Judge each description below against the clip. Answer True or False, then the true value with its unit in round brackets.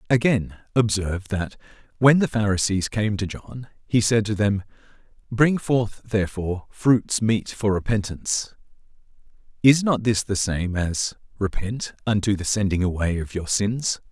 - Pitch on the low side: True (105 Hz)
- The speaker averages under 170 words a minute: True (145 wpm)